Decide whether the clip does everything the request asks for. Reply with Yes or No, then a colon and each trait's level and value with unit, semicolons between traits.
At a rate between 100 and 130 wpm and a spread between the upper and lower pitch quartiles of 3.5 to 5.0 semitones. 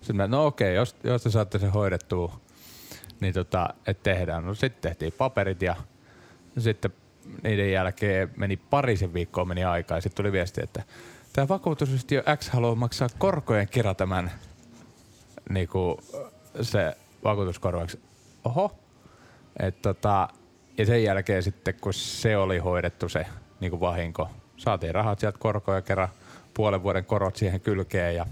No: average, 145 wpm; average, 4.1 semitones